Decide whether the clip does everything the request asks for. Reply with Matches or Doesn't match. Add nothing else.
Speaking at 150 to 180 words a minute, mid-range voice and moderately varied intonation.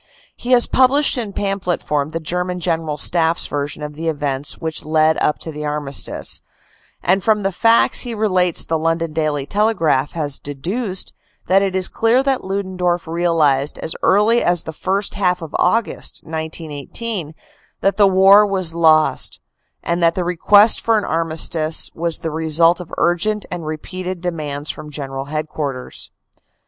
Matches